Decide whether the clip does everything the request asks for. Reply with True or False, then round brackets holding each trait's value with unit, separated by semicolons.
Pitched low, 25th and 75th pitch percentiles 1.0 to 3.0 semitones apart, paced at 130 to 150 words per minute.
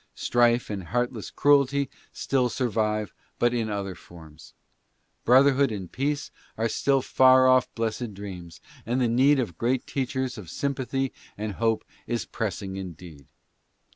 False (120 Hz; 4.3 semitones; 140 wpm)